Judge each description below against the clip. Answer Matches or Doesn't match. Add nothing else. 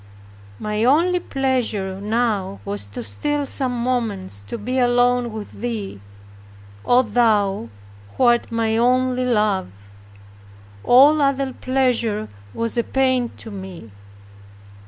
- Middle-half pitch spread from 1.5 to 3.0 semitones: Doesn't match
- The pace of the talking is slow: Matches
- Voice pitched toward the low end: Doesn't match